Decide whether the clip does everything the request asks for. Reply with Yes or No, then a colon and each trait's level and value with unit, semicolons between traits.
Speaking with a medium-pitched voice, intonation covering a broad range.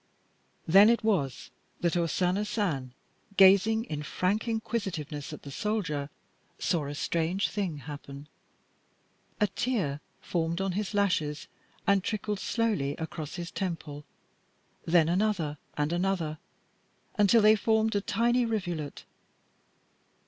Yes: medium, 180 Hz; wide, 5.7 semitones